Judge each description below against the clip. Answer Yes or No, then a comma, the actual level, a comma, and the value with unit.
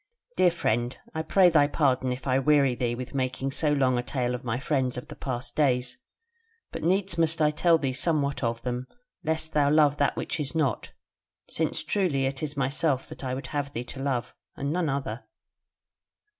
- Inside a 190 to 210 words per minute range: Yes, average, 200 wpm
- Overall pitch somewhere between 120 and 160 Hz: Yes, medium, 140 Hz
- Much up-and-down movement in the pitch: No, average, 3.3 semitones